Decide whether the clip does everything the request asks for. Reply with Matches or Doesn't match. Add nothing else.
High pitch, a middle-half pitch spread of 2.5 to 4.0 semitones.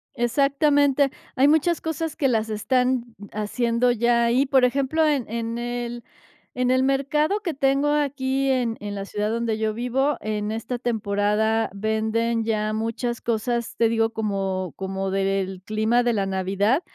Matches